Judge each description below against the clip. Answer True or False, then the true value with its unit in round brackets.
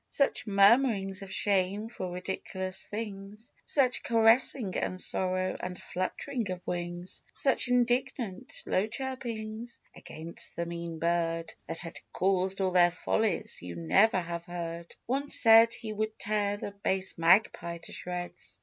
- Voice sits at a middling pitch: False (195 Hz)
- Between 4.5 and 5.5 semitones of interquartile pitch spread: False (4.0 semitones)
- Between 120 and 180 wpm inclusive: True (140 wpm)